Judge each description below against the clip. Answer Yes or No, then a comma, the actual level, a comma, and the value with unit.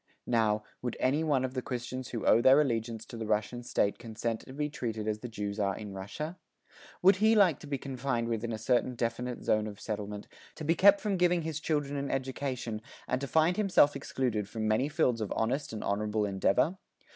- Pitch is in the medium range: No, low, 125 Hz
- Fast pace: Yes, fast, 210 wpm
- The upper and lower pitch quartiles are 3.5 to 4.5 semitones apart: No, average, 4.9 semitones